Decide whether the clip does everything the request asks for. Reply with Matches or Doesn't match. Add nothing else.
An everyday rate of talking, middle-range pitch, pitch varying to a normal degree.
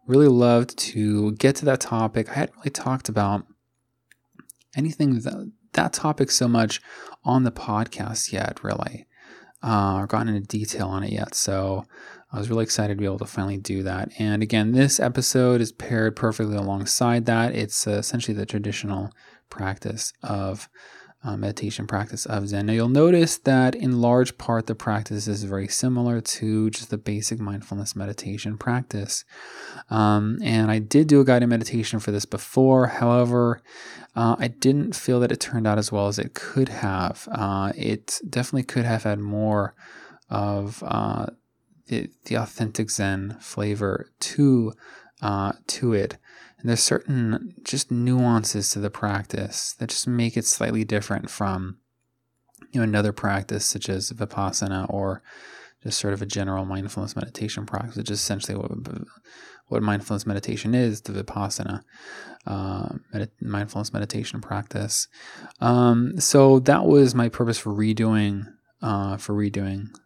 Doesn't match